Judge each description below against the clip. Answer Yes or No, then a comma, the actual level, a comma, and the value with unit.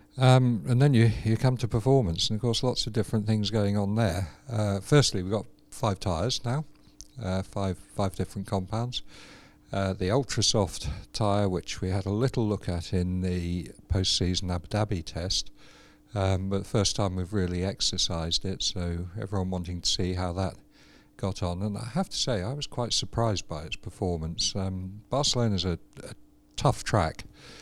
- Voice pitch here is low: Yes, low, 100 Hz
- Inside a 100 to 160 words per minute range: No, average, 185 wpm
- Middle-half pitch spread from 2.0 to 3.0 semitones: No, average, 3.7 semitones